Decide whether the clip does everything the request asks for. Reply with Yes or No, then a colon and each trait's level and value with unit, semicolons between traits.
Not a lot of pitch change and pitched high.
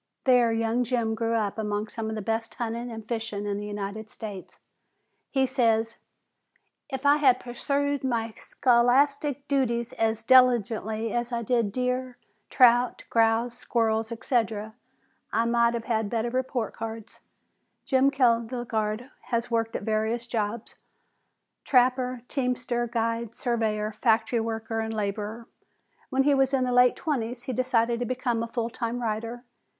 Yes: narrow, 2.0 semitones; high, 235 Hz